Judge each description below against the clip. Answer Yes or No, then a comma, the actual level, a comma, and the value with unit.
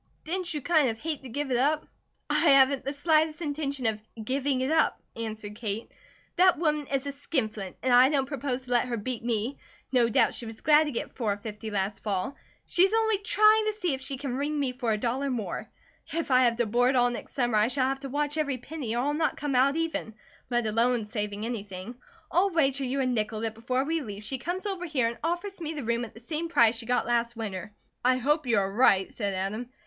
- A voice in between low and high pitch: No, very high, 255 Hz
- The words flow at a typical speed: No, fast, 235 wpm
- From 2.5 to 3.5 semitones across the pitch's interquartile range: No, average, 4.7 semitones